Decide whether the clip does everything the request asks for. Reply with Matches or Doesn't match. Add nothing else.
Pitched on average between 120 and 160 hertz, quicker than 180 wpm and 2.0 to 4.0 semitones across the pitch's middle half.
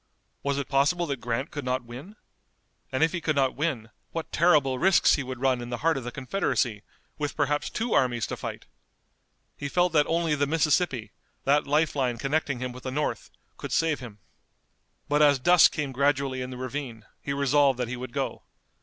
Matches